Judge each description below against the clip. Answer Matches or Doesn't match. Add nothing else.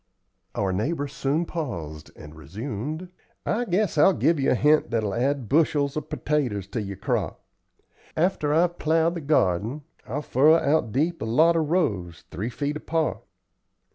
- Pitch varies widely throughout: Matches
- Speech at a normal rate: Matches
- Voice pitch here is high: Doesn't match